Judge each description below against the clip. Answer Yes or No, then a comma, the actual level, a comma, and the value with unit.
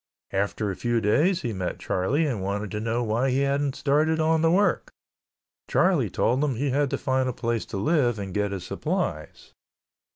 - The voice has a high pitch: No, low, 125 Hz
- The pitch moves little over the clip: No, wide, 5.6 semitones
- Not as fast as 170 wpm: No, average, 195 wpm